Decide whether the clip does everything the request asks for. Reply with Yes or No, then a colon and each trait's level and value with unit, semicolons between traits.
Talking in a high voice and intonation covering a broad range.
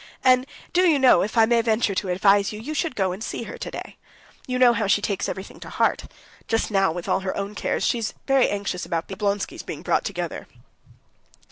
No: high, 210 Hz; average, 3.8 semitones